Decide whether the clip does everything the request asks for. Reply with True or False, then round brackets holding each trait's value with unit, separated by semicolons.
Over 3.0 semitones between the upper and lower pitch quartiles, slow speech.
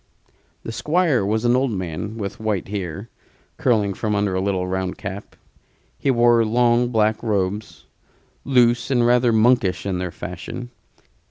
False (3.8 semitones; 150 wpm)